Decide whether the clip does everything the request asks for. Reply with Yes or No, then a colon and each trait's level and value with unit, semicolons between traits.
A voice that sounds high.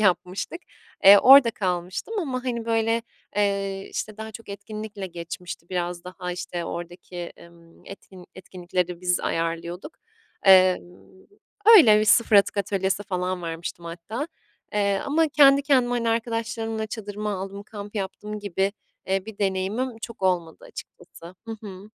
Yes: high, 200 Hz